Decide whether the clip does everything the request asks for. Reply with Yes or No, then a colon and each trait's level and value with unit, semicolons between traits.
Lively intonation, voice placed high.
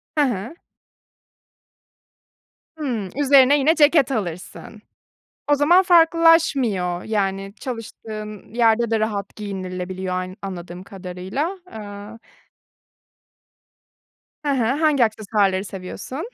Yes: wide, 6.4 semitones; high, 220 Hz